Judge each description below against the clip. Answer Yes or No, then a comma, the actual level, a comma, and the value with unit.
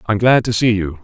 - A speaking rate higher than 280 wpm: Yes, fast, 350 wpm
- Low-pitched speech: Yes, low, 110 Hz